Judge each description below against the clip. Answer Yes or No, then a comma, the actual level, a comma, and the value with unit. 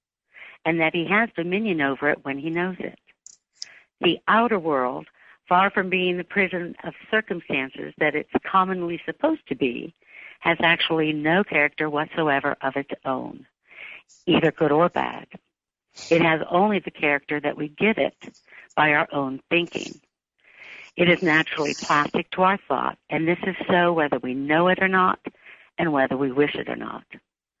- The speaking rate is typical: Yes, average, 165 wpm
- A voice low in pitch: No, medium, 165 Hz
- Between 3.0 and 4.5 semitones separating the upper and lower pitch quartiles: Yes, average, 3.7 semitones